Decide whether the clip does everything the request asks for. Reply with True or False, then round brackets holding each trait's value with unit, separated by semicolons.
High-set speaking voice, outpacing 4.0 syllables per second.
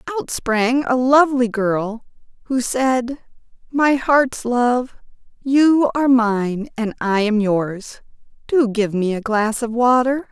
False (240 Hz; 3.5 syllables/s)